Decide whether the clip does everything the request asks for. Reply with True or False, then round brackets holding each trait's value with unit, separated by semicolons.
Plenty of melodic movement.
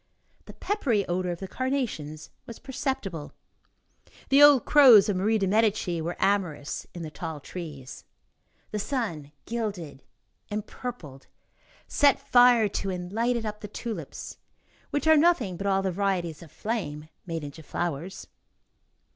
True (6.0 semitones)